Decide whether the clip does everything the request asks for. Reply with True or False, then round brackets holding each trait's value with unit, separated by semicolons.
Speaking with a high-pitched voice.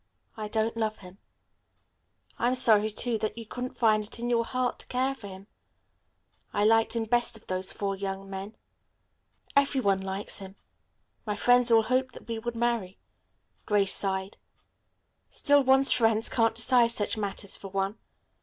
True (220 Hz)